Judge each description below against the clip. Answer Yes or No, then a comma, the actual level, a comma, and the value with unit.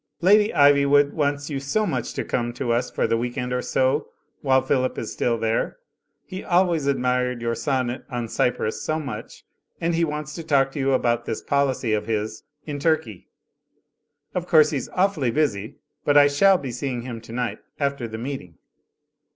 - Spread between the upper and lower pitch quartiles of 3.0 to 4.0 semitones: Yes, average, 3.7 semitones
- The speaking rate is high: No, average, 185 wpm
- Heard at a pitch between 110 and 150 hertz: Yes, low, 135 Hz